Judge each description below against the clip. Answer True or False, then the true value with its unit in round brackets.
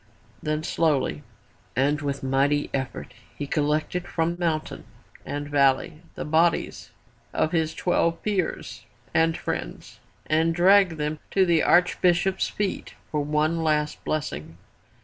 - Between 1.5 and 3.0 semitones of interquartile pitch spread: True (2.6 semitones)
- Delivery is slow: True (125 wpm)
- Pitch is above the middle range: False (155 Hz)